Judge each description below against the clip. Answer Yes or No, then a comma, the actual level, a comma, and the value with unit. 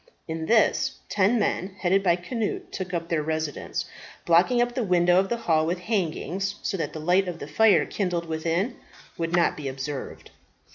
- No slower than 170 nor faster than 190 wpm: Yes, average, 185 wpm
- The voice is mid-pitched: Yes, medium, 175 Hz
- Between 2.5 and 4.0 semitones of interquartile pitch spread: Yes, average, 3.4 semitones